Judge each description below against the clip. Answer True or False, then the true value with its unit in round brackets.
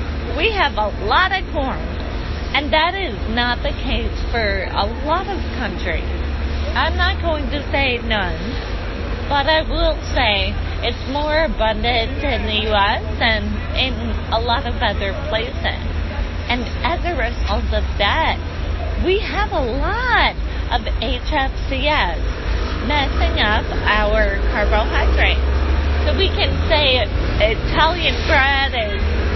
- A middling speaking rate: False (130 wpm)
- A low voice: True (80 Hz)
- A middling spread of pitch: False (2.1 semitones)